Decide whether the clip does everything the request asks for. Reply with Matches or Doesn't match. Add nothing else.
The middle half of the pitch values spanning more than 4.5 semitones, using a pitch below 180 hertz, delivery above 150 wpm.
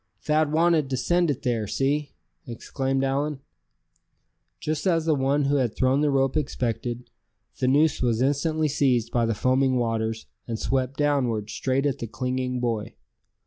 Doesn't match